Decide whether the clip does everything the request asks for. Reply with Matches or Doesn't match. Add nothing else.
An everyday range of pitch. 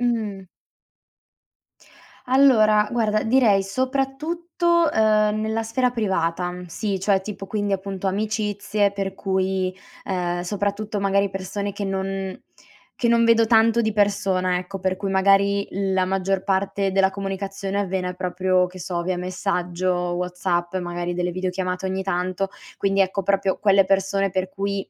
Doesn't match